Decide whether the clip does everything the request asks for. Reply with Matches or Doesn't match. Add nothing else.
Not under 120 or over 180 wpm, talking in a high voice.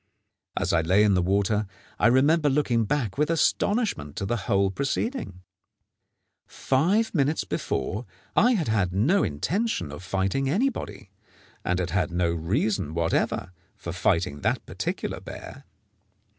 Doesn't match